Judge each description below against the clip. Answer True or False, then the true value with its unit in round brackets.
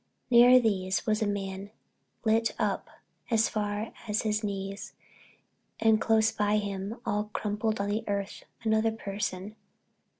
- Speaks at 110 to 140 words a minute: True (135 wpm)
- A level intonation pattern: True (1.7 semitones)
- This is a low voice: False (210 Hz)